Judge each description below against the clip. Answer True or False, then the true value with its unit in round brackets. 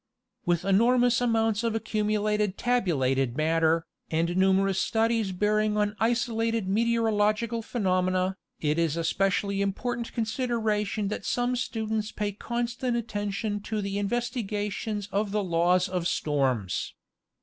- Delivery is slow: True (125 wpm)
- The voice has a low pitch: False (210 Hz)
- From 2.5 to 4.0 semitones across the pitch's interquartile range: True (3.4 semitones)